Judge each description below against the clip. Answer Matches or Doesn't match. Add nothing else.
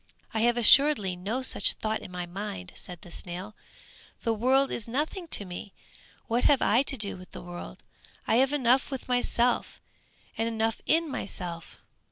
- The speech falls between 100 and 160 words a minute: Doesn't match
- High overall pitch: Matches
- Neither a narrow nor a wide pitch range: Doesn't match